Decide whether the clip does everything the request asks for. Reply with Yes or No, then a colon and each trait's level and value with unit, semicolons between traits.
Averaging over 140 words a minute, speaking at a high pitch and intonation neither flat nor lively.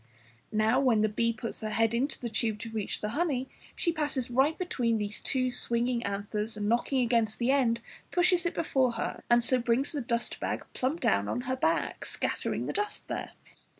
Yes: average, 200 wpm; high, 240 Hz; average, 3.2 semitones